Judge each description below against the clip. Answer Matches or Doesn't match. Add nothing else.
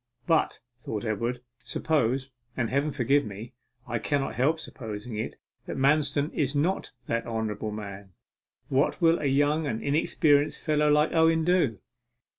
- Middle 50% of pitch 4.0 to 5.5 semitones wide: Matches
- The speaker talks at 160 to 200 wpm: Doesn't match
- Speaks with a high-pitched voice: Doesn't match